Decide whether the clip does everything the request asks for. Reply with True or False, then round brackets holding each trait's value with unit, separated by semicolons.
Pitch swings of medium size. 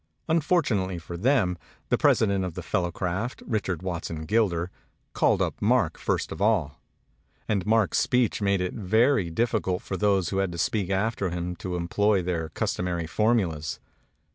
True (3.8 semitones)